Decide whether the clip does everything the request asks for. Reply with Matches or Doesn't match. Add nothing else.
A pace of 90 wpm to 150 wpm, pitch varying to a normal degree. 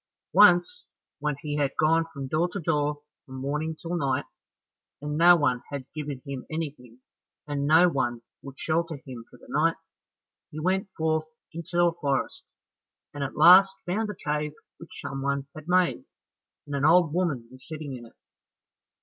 Doesn't match